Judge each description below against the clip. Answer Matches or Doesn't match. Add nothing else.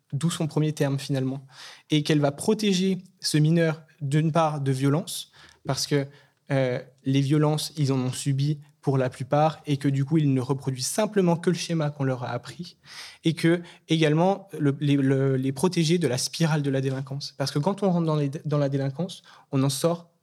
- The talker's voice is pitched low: Doesn't match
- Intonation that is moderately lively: Matches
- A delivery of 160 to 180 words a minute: Doesn't match